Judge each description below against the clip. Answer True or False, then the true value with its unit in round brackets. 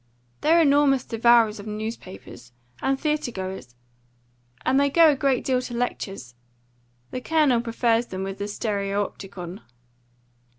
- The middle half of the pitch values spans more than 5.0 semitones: True (5.5 semitones)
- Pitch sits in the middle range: False (230 Hz)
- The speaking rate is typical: False (130 wpm)